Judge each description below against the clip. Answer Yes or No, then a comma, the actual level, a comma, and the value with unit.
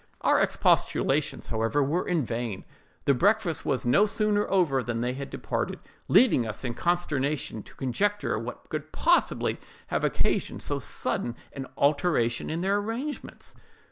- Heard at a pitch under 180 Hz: Yes, medium, 140 Hz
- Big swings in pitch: Yes, wide, 8.2 semitones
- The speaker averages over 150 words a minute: No, average, 140 wpm